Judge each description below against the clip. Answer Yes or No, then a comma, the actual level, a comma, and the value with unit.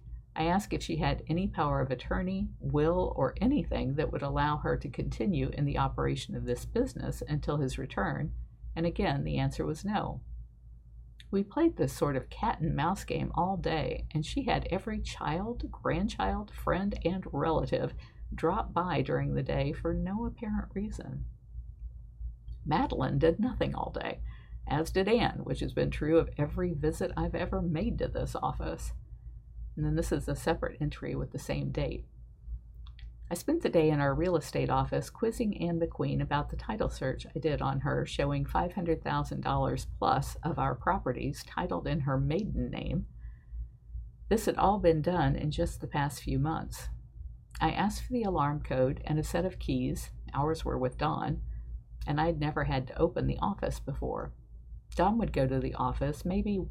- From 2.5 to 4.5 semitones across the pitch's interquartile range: No, average, 5.0 semitones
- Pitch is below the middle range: No, medium, 150 Hz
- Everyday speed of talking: Yes, average, 175 wpm